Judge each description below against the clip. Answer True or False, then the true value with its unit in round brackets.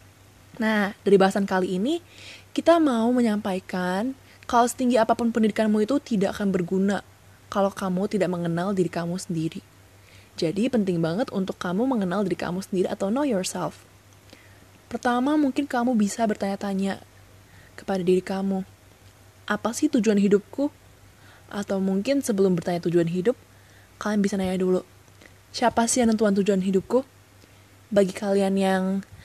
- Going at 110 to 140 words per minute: True (135 wpm)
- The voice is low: False (195 Hz)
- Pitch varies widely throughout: False (4.2 semitones)